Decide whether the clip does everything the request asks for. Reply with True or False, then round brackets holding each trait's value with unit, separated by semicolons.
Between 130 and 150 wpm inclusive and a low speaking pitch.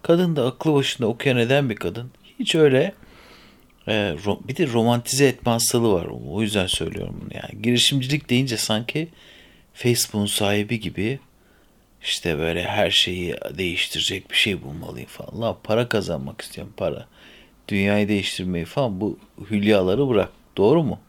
True (140 wpm; 115 Hz)